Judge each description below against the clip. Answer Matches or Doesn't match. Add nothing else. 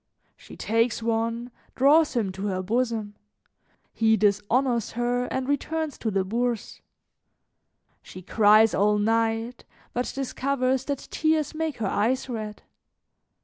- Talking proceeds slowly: Matches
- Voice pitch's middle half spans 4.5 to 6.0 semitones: Doesn't match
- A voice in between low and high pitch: Doesn't match